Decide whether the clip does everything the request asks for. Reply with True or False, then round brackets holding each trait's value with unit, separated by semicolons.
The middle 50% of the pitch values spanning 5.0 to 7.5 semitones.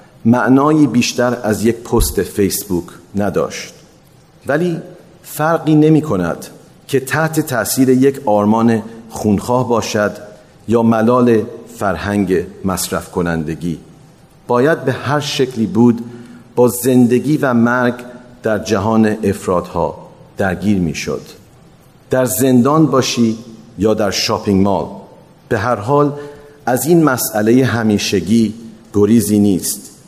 False (3.9 semitones)